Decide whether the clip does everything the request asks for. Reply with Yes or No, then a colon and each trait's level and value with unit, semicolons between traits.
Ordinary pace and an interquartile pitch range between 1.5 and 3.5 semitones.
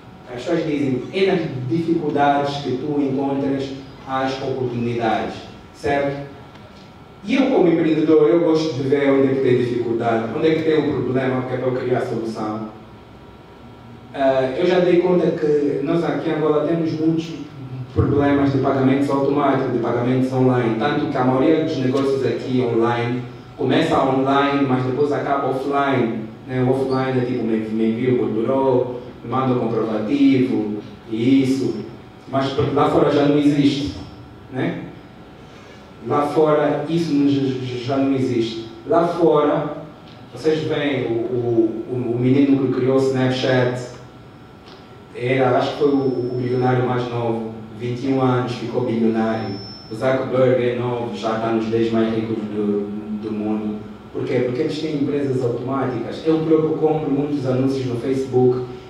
Yes: average, 150 wpm; average, 2.9 semitones